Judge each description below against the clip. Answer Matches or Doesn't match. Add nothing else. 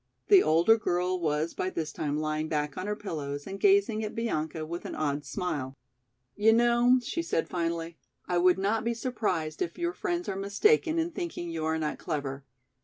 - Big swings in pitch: Matches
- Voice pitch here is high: Doesn't match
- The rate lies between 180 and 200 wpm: Matches